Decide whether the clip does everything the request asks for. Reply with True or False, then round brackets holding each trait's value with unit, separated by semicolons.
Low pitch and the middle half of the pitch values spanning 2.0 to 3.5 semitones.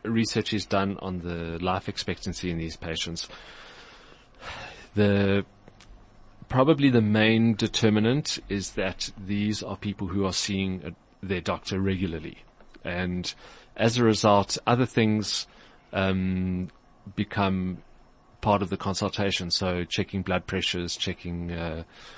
True (100 Hz; 2.5 semitones)